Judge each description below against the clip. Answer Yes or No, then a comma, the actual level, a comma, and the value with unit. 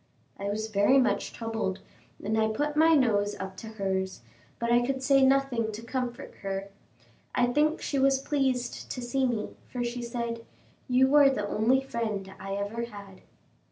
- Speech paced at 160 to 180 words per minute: Yes, average, 175 wpm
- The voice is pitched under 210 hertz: No, high, 235 Hz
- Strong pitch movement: No, average, 4.3 semitones